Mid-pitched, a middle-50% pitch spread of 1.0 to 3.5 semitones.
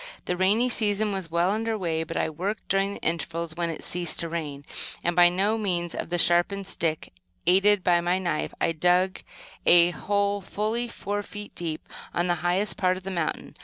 Yes: medium, 180 Hz; average, 3.0 semitones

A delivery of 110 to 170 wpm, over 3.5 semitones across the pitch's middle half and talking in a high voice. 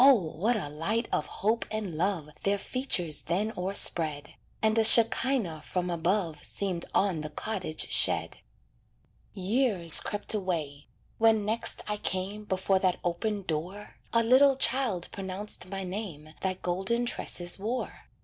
Yes: average, 140 wpm; average, 4.2 semitones; high, 195 Hz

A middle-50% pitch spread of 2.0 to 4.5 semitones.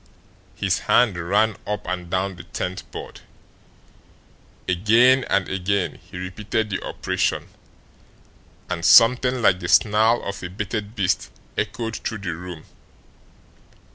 Yes: average, 3.4 semitones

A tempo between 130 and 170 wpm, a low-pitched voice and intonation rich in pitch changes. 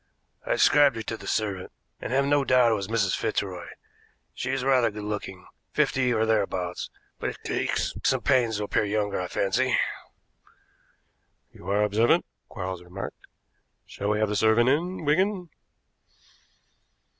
No: average, 150 wpm; low, 110 Hz; average, 4.4 semitones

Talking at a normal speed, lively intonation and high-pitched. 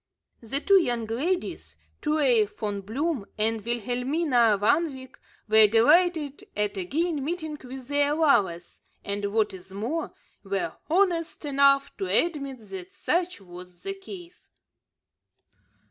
No: slow, 125 wpm; wide, 7.1 semitones; very high, 260 Hz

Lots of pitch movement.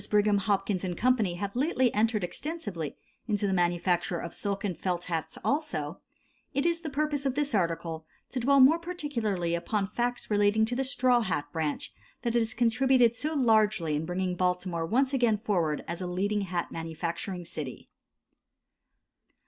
Yes: wide, 6.1 semitones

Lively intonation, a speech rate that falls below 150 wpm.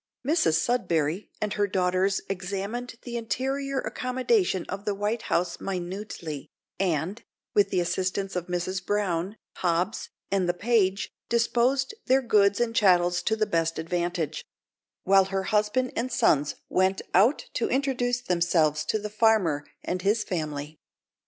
No: average, 4.4 semitones; average, 140 wpm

